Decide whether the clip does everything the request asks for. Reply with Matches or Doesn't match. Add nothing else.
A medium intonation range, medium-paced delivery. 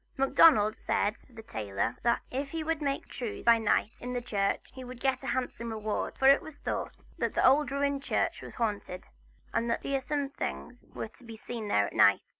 Doesn't match